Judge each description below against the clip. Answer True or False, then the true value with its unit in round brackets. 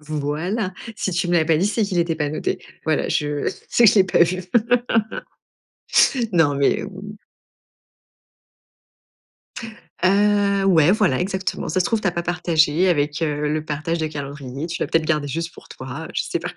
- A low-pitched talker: False (165 Hz)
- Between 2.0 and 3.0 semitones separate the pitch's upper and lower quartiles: False (3.8 semitones)